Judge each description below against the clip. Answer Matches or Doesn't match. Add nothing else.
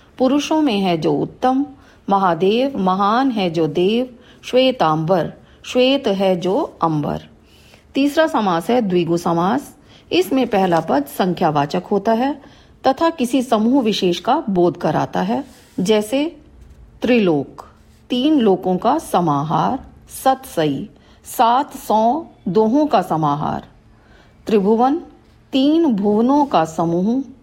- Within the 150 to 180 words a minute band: Doesn't match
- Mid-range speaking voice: Doesn't match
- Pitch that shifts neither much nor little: Doesn't match